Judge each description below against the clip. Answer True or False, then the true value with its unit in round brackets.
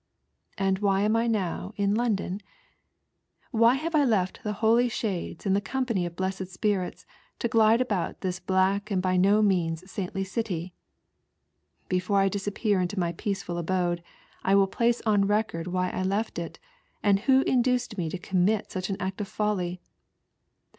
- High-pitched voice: True (195 Hz)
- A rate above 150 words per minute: True (170 wpm)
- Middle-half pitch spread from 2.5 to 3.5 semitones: True (2.9 semitones)